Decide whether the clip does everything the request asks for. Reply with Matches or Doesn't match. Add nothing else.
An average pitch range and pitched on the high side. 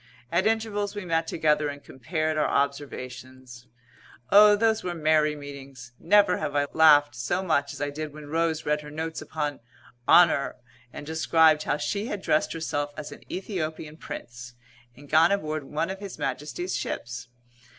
Doesn't match